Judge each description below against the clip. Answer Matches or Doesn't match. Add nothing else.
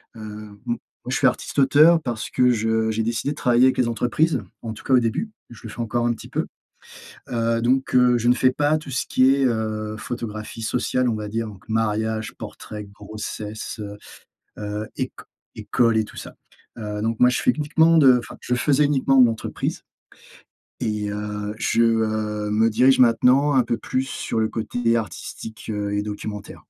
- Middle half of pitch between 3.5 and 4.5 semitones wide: Doesn't match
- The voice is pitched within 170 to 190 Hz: Doesn't match